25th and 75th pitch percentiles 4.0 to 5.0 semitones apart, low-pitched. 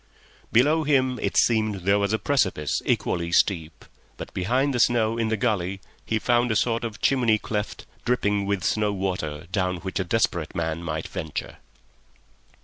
Yes: average, 4.3 semitones; low, 105 Hz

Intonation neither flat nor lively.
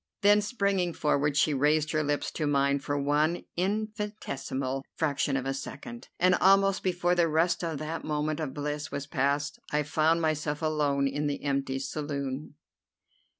Yes: average, 3.4 semitones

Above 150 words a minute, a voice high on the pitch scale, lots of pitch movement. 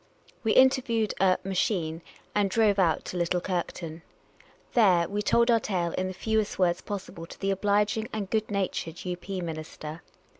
No: average, 175 wpm; high, 195 Hz; average, 3.7 semitones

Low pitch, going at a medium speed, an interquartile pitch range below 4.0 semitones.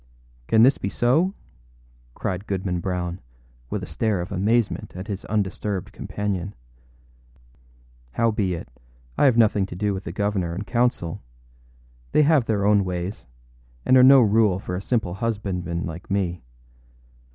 Yes: low, 100 Hz; average, 150 wpm; average, 3.6 semitones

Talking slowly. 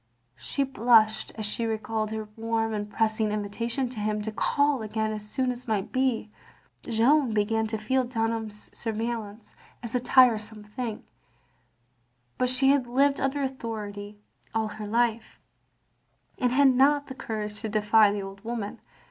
No: average, 150 wpm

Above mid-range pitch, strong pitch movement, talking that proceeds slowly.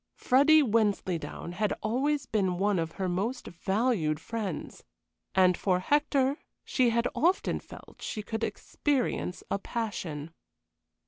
Yes: high, 215 Hz; wide, 5.9 semitones; slow, 125 wpm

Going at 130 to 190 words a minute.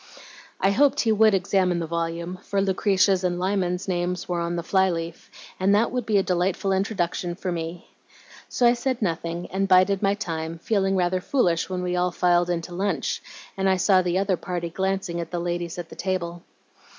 No: average, 200 wpm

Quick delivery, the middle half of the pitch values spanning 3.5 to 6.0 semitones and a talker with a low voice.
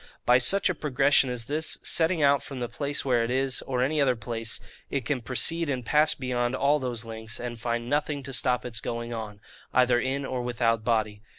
No: fast, 210 wpm; average, 3.0 semitones; low, 125 Hz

